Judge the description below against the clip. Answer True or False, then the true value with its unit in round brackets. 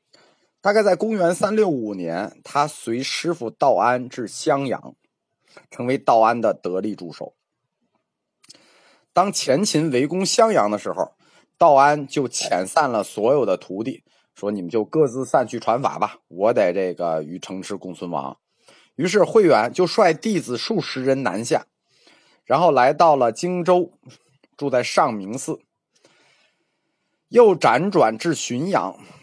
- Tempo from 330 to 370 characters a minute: False (205 characters per minute)